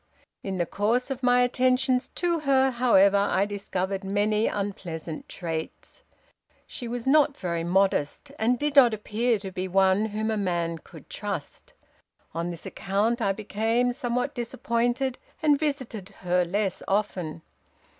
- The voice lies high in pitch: Yes, high, 215 Hz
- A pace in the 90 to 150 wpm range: Yes, average, 145 wpm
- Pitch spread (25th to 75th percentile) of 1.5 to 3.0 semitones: No, average, 4.6 semitones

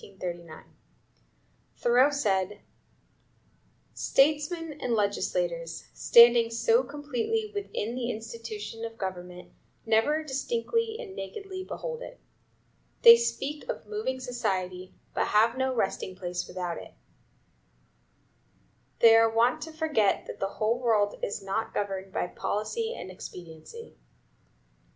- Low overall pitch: No, high, 235 Hz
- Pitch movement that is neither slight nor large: No, wide, 7.6 semitones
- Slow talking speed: Yes, slow, 110 wpm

